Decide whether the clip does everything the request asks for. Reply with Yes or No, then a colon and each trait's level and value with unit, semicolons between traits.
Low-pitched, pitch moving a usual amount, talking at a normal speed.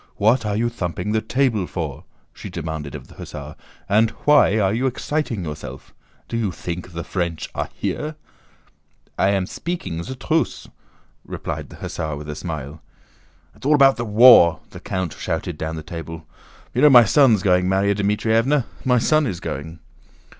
No: low, 100 Hz; wide, 6.2 semitones; average, 170 wpm